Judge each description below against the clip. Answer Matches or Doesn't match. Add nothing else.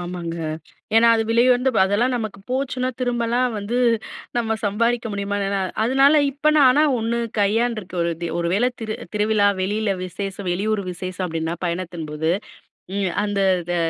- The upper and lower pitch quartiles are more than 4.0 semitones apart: Matches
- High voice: Matches